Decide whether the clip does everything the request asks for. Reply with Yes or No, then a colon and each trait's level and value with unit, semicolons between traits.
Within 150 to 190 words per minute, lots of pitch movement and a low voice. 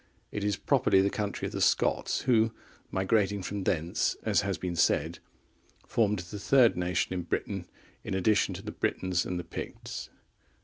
No: average, 170 wpm; narrow, 2.6 semitones; very low, 95 Hz